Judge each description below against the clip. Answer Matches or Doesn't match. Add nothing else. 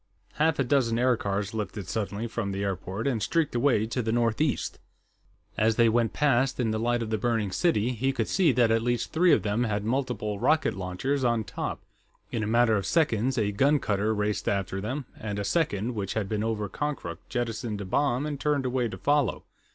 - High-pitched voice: Doesn't match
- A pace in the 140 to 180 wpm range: Doesn't match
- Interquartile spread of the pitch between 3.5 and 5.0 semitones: Matches